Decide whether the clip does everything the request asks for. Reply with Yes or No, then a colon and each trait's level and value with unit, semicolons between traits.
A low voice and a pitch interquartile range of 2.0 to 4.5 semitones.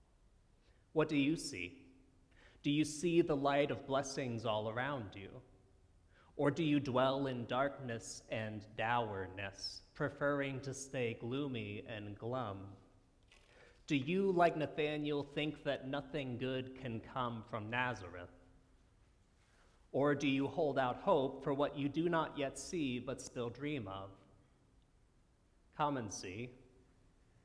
No: low, 130 Hz; average, 5.0 semitones